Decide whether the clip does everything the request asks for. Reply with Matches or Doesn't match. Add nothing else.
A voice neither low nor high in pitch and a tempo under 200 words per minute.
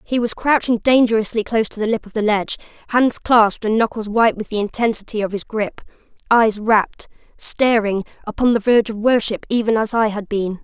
Doesn't match